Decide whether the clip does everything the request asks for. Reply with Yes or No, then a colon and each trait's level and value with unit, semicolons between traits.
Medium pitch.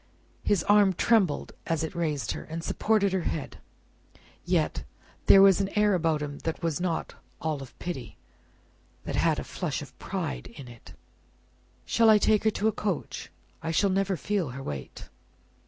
Yes: medium, 175 Hz